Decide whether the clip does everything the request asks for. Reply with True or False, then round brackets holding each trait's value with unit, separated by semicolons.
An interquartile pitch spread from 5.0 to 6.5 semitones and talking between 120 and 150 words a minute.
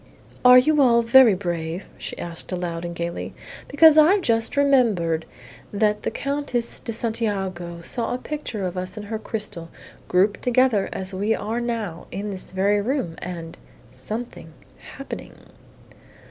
True (5.3 semitones; 145 wpm)